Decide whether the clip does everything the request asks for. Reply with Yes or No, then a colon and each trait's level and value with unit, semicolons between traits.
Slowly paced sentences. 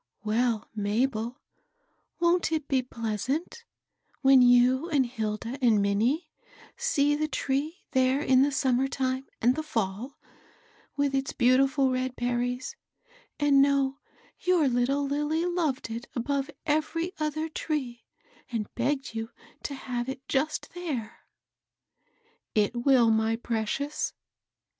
Yes: slow, 130 wpm